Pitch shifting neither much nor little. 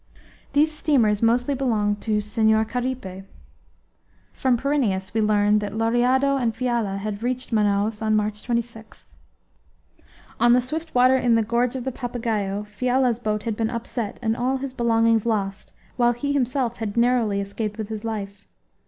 Yes: average, 3.0 semitones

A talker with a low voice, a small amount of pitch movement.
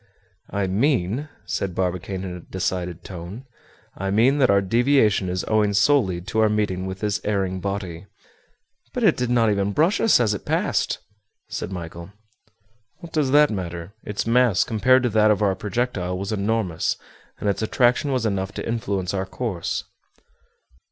No: low, 100 Hz; average, 4.0 semitones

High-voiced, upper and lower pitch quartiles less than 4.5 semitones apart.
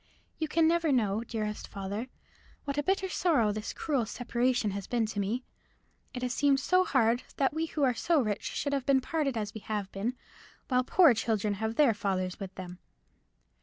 No: high, 240 Hz; average, 5.2 semitones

